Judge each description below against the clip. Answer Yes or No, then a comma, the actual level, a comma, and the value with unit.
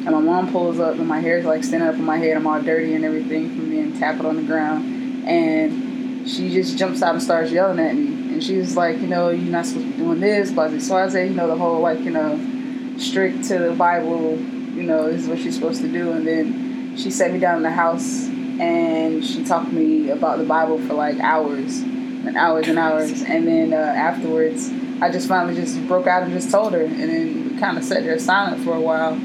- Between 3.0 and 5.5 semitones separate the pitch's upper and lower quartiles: No, narrow, 2.5 semitones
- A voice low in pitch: No, very high, 260 Hz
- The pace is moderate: No, fast, 250 wpm